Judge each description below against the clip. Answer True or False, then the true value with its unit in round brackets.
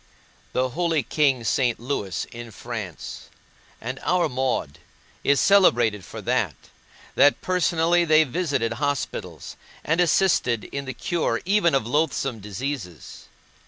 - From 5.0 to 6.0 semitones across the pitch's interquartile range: True (5.6 semitones)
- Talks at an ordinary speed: False (125 wpm)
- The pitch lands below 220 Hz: True (135 Hz)